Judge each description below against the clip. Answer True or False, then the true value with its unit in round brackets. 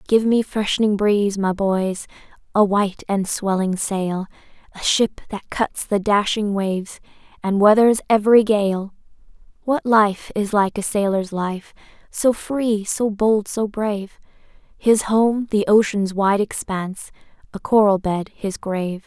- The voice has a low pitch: False (205 Hz)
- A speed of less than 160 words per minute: True (145 wpm)